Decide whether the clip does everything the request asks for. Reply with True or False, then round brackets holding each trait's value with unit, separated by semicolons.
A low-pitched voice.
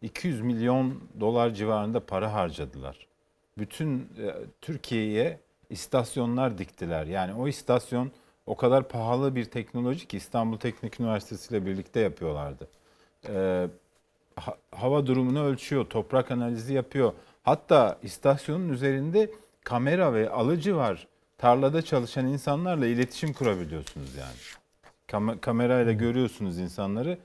True (120 Hz)